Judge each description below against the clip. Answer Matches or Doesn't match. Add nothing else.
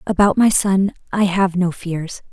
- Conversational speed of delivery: Matches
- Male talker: Doesn't match